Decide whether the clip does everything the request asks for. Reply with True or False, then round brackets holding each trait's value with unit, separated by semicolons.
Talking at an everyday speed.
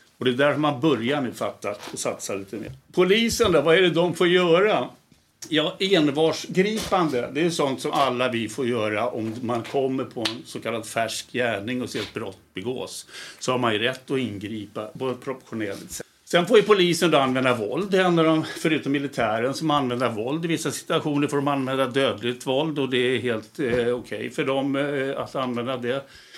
False (205 wpm)